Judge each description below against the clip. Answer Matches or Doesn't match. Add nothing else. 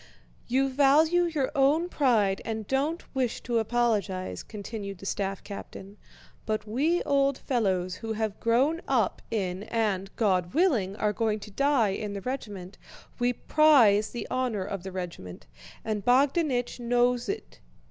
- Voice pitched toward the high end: Matches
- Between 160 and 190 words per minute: Doesn't match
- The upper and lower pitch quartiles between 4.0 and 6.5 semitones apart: Matches